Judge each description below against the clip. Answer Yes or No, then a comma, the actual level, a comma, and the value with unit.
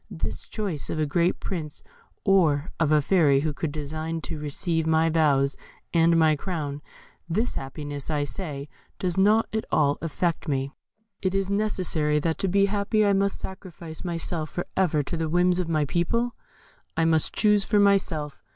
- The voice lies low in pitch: No, medium, 165 Hz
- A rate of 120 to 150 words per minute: No, average, 175 wpm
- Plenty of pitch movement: No, average, 4.1 semitones